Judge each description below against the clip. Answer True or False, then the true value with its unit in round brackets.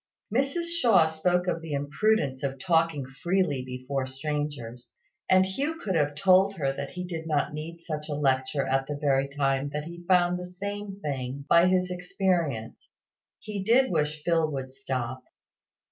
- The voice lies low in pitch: False (155 Hz)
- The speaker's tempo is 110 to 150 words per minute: False (165 wpm)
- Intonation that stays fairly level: False (4.8 semitones)